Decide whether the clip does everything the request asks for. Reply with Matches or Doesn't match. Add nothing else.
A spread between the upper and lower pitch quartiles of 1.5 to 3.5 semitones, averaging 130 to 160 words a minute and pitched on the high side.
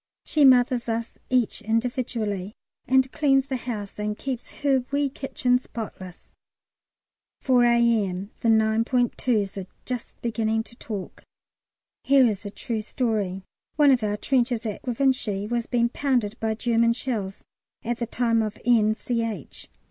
Matches